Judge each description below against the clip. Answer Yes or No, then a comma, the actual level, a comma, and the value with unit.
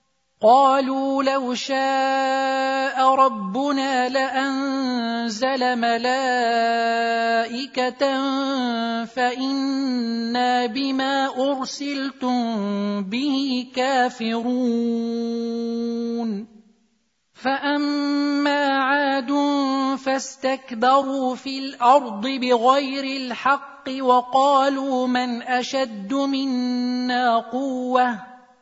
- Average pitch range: No, narrow, 2.1 semitones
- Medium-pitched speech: No, very high, 260 Hz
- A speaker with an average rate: No, slow, 50 wpm